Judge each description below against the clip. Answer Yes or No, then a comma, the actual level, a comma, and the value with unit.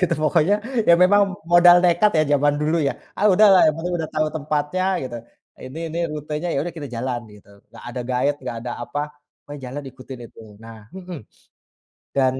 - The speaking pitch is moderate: Yes, medium, 150 Hz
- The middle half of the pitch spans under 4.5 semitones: No, average, 5.0 semitones